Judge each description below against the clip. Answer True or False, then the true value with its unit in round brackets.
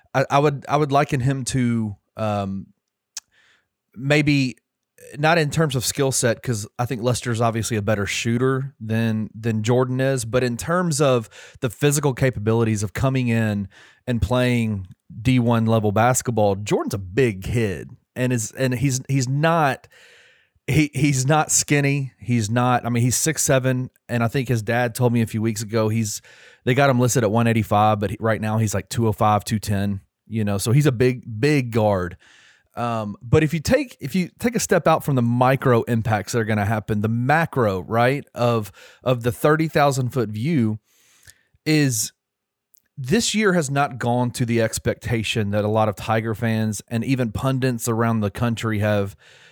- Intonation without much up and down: False (3.5 semitones)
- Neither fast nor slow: True (180 wpm)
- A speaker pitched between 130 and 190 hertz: False (120 Hz)